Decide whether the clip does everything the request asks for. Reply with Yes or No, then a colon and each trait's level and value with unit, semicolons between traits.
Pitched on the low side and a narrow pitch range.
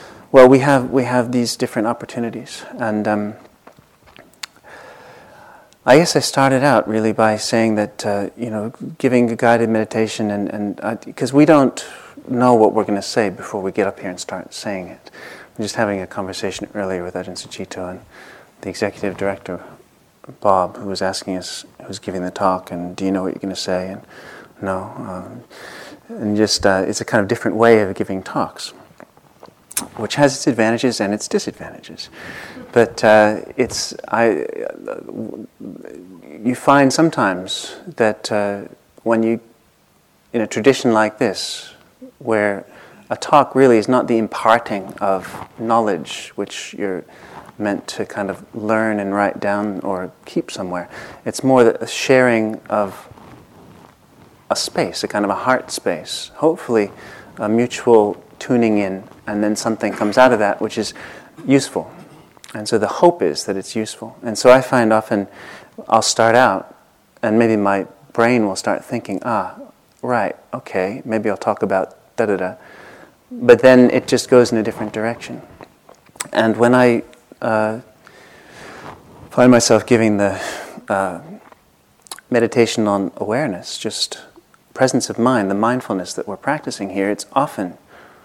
No: low, 110 Hz; average, 3.4 semitones